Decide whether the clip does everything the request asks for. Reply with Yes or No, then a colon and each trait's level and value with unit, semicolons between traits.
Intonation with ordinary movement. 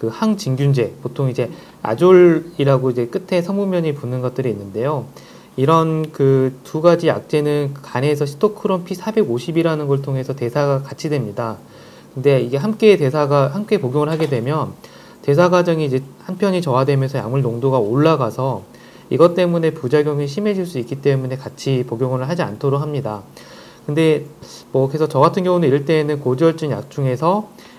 Yes: average, 4.2 semitones